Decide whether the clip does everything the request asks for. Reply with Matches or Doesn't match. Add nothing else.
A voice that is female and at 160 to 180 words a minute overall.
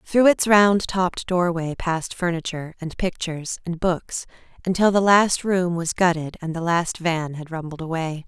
Matches